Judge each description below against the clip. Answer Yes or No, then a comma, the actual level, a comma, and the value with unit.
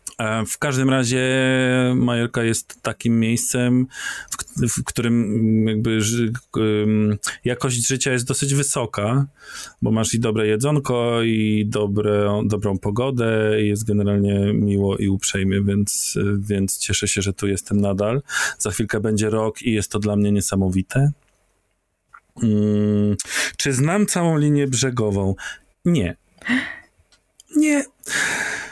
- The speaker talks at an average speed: Yes, average, 120 wpm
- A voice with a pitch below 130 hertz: Yes, low, 110 Hz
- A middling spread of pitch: Yes, average, 3.6 semitones